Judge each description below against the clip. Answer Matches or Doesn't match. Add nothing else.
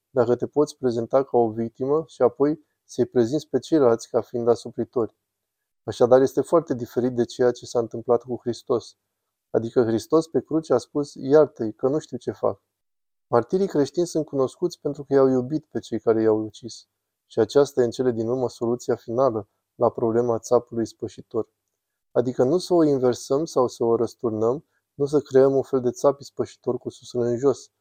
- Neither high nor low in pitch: Doesn't match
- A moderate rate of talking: Doesn't match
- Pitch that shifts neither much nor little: Matches